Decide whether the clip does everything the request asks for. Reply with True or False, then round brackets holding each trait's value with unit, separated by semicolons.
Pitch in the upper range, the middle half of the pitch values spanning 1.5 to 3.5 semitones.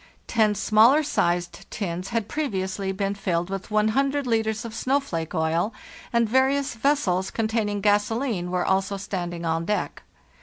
False (210 Hz; 4.1 semitones)